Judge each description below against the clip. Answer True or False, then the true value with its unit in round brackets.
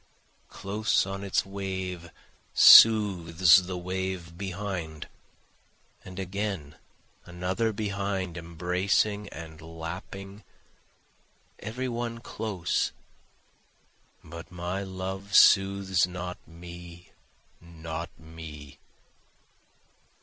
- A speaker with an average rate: False (75 wpm)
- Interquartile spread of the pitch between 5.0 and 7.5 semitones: False (2.6 semitones)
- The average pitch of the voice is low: True (95 Hz)